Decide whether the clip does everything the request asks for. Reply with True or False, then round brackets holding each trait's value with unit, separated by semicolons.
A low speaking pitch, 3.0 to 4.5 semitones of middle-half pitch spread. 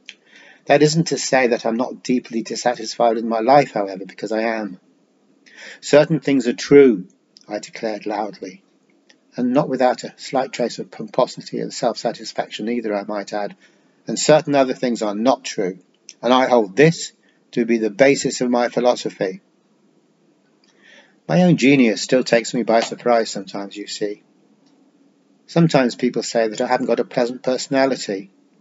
True (120 Hz; 3.8 semitones)